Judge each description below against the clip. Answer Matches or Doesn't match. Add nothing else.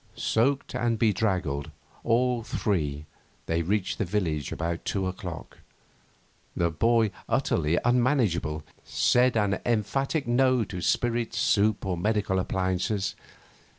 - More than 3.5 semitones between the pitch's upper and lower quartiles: Matches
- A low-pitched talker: Matches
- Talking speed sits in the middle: Doesn't match